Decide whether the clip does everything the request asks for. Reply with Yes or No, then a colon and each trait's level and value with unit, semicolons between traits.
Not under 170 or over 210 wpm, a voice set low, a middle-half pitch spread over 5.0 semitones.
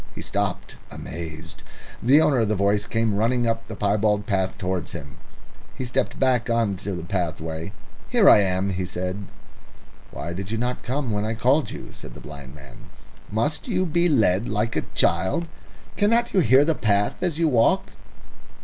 Yes: average, 175 wpm; low, 105 Hz; wide, 5.5 semitones